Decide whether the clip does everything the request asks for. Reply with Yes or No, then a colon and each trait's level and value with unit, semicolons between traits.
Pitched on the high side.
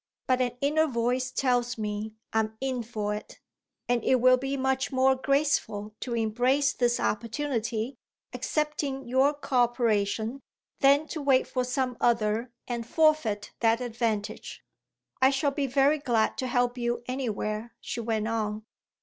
Yes: high, 245 Hz